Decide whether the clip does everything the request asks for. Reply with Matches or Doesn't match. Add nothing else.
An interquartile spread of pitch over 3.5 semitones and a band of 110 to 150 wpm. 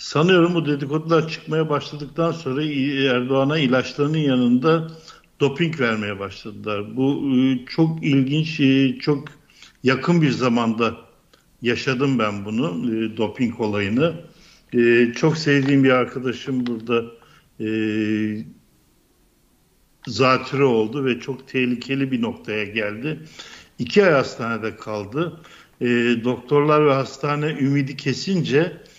Doesn't match